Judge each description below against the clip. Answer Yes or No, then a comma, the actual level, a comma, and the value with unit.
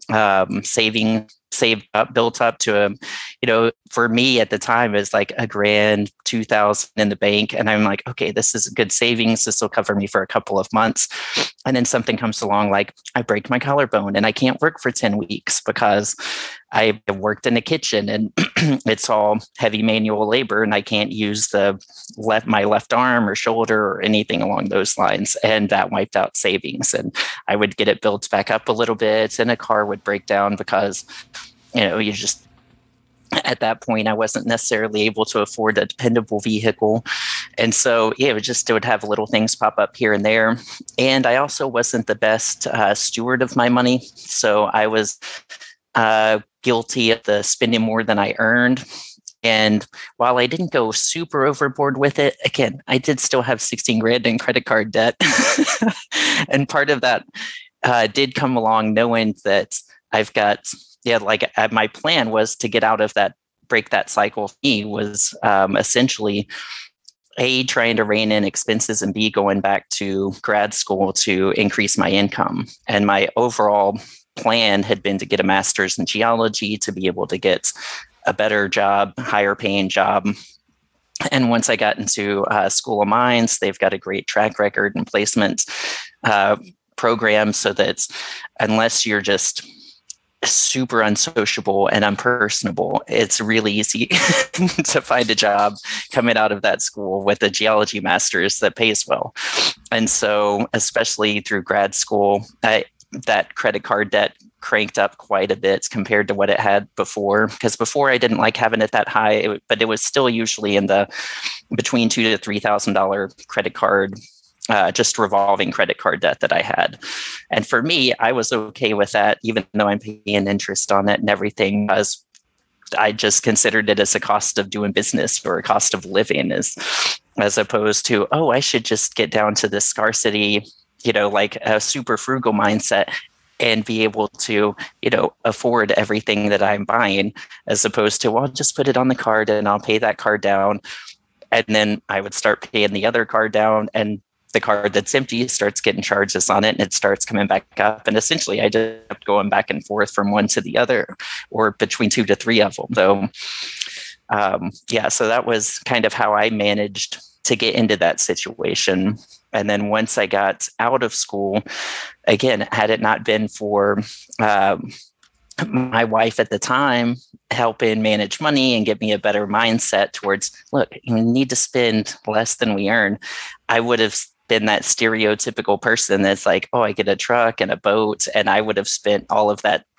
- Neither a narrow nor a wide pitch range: No, narrow, 2.2 semitones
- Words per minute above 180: Yes, average, 190 wpm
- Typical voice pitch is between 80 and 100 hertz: No, low, 110 Hz